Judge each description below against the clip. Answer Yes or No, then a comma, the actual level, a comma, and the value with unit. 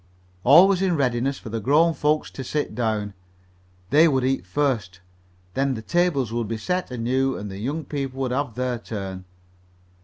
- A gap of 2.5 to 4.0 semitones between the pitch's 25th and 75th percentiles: No, average, 4.4 semitones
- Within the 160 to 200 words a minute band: Yes, average, 180 wpm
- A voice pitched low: Yes, low, 130 Hz